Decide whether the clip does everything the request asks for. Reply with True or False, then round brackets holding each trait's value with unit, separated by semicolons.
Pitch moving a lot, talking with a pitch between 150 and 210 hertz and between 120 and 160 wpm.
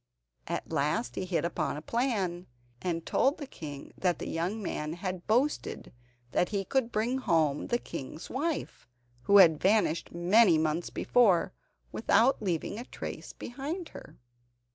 True (6.2 semitones; 185 Hz; 150 wpm)